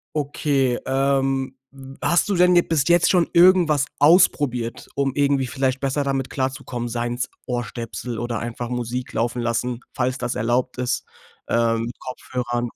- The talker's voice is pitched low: Yes, low, 130 Hz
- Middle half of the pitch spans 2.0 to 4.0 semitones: Yes, narrow, 2.6 semitones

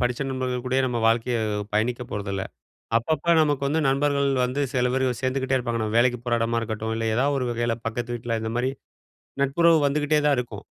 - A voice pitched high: No, low, 125 Hz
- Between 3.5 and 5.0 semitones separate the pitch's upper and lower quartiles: No, average, 2.9 semitones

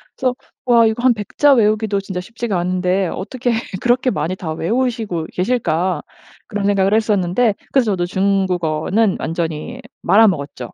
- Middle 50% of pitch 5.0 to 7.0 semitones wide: No, average, 4.4 semitones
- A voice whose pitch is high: Yes, high, 200 Hz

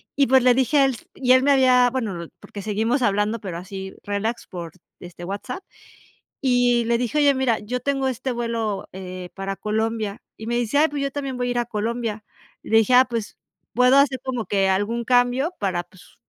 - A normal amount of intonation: Yes, average, 3.9 semitones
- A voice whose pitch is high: Yes, high, 235 Hz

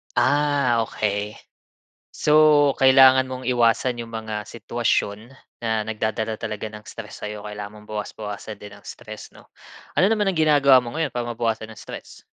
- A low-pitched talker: Yes, low, 115 Hz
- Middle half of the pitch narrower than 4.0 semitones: Yes, average, 3.6 semitones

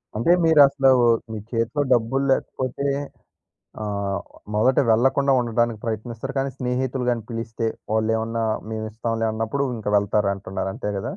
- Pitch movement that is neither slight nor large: Yes, average, 3.1 semitones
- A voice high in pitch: No, low, 115 Hz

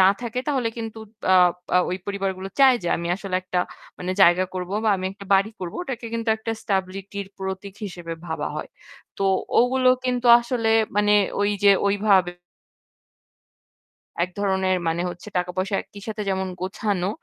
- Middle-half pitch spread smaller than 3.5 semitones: Yes, average, 2.9 semitones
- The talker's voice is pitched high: Yes, high, 195 Hz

